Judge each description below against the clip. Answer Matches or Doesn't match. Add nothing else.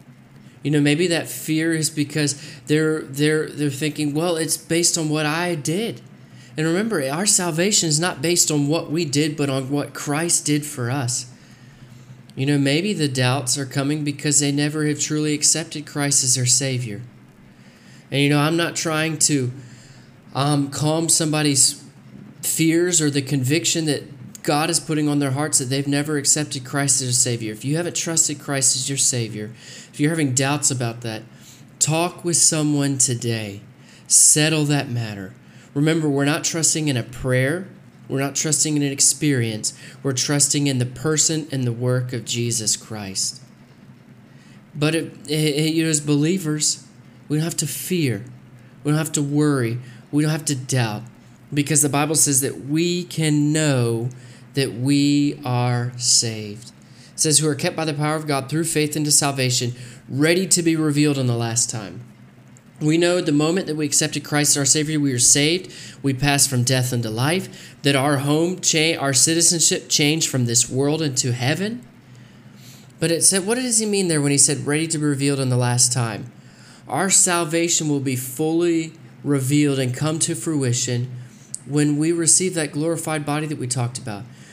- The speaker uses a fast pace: Doesn't match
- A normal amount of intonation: Matches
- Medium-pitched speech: Matches